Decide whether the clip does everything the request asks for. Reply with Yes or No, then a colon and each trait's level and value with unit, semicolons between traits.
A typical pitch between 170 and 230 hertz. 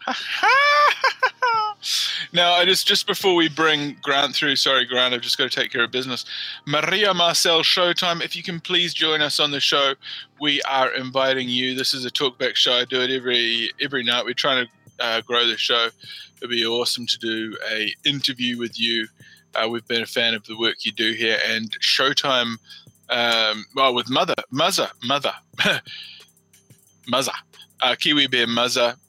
No: low, 130 Hz